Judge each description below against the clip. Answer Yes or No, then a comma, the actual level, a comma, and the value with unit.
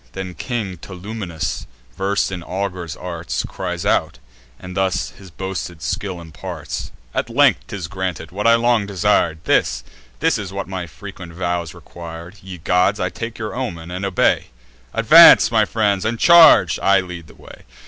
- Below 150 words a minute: No, average, 160 wpm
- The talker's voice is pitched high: No, very low, 95 Hz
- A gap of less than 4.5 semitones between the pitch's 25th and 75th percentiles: Yes, average, 2.8 semitones